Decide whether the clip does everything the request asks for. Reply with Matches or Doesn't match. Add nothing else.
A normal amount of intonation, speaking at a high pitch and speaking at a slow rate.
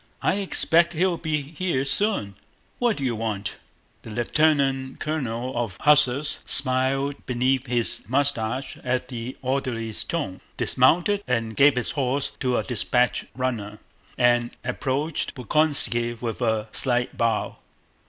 Doesn't match